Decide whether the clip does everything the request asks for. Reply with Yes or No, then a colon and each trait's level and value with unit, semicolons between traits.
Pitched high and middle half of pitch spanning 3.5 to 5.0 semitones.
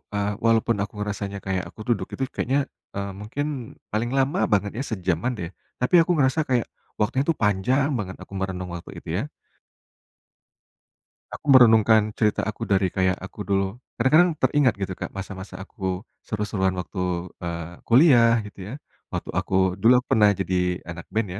No: low, 105 Hz; average, 4.4 semitones